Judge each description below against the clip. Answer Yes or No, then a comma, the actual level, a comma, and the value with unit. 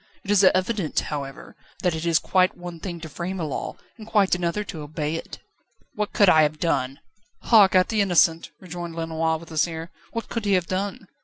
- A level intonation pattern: No, average, 3.1 semitones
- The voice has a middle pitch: Yes, medium, 175 Hz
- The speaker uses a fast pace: Yes, fast, 210 wpm